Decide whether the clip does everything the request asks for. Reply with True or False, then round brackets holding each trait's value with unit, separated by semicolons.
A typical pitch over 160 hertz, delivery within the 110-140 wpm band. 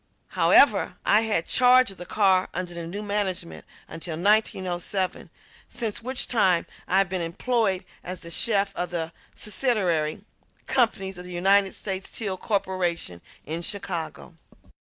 True (190 Hz; 135 wpm)